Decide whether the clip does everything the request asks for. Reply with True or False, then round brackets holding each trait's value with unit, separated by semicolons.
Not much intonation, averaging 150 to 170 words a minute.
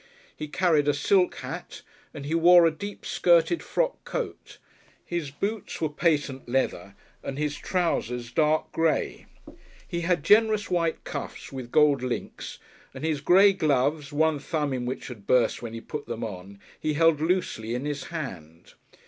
False (4.8 semitones; 165 wpm)